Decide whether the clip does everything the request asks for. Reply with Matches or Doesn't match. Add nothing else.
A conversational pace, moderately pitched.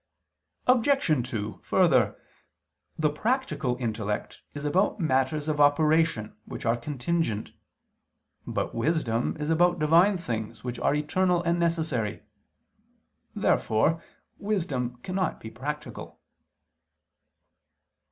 Doesn't match